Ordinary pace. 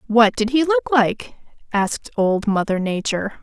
Yes: average, 160 wpm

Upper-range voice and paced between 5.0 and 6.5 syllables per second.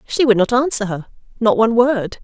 Yes: high, 225 Hz; 5.8 syllables/s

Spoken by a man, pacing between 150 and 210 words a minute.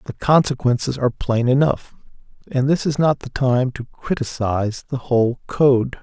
Yes: male; average, 160 wpm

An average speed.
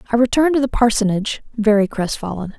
Yes: average, 165 wpm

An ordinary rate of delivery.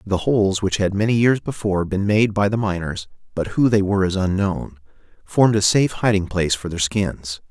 Yes: average, 190 wpm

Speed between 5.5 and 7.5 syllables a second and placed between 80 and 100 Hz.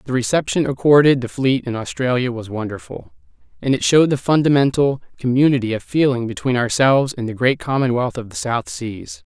No: 5.6 syllables/s; low, 130 Hz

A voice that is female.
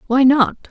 Yes: female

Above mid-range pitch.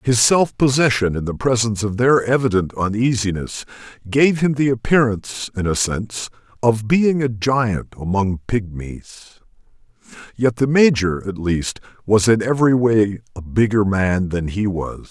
No: low, 110 Hz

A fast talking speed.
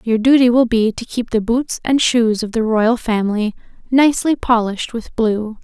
No: average, 190 wpm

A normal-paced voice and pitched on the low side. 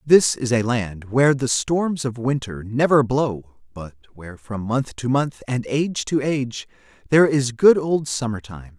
Yes: average, 185 wpm; low, 125 Hz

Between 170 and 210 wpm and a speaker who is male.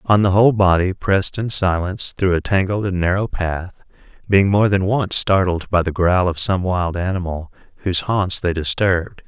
Yes: average, 190 wpm; male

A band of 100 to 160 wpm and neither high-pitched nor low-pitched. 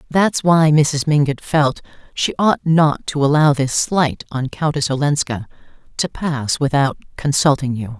Yes: average, 150 wpm; medium, 145 Hz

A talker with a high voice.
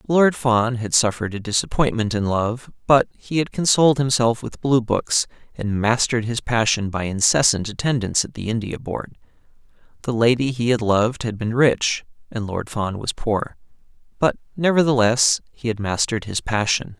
No: low, 115 Hz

